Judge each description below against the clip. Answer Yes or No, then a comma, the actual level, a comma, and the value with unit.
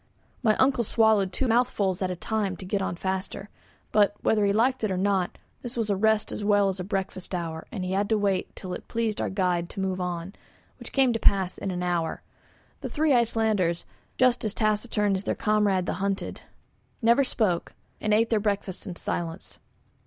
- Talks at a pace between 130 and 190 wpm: No, fast, 205 wpm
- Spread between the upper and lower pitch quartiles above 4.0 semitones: No, average, 2.9 semitones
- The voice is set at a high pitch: Yes, high, 200 Hz